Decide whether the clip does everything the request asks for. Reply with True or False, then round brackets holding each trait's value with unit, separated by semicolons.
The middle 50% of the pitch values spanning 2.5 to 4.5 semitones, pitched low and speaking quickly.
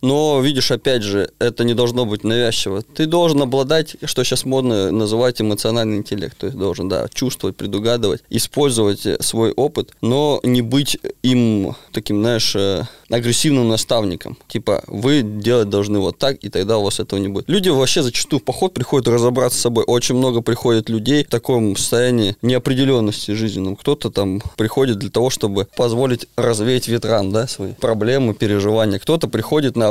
True (3.6 semitones; 120 Hz; 165 wpm)